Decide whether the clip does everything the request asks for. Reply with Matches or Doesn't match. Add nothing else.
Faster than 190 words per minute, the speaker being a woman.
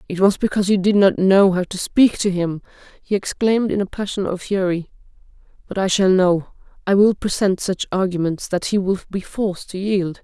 Matches